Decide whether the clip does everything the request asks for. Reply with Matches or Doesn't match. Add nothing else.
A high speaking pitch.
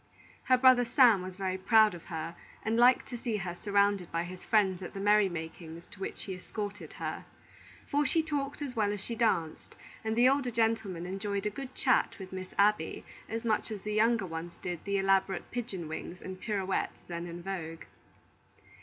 Matches